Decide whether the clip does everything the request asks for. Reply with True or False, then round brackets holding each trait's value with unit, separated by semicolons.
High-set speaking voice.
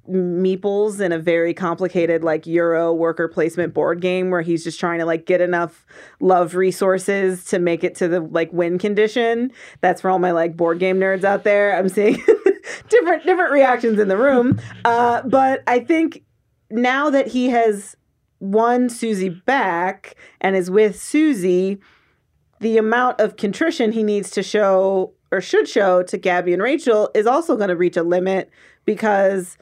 True (195 Hz)